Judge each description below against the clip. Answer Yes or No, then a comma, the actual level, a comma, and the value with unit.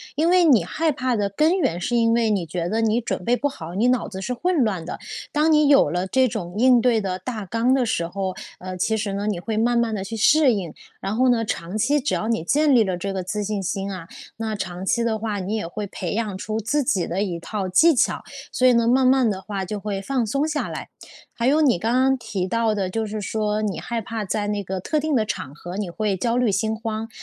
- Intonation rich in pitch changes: No, average, 4.3 semitones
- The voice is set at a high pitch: Yes, high, 220 Hz